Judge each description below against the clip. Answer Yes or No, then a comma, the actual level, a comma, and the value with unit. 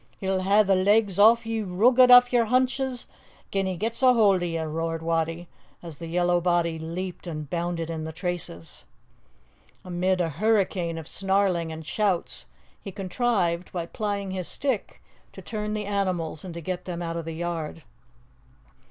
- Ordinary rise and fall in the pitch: Yes, average, 3.7 semitones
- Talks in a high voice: No, medium, 180 Hz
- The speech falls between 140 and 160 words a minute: No, average, 170 wpm